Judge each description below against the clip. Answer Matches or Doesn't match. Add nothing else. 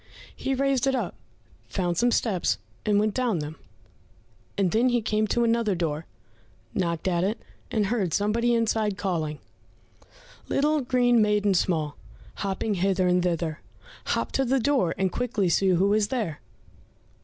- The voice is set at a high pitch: Matches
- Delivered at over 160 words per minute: Doesn't match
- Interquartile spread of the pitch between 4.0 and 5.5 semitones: Matches